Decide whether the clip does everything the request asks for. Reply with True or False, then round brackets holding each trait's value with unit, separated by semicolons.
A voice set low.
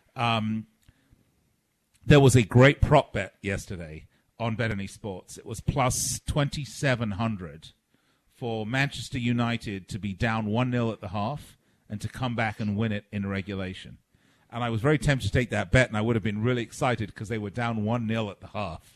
True (115 Hz)